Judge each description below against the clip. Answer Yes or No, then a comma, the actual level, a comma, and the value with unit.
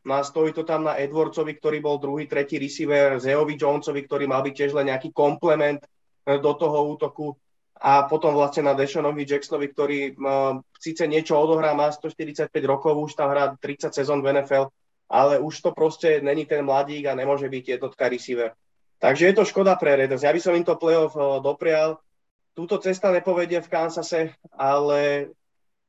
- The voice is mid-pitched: Yes, medium, 145 Hz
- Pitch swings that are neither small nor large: No, narrow, 2.1 semitones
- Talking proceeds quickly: Yes, fast, 175 wpm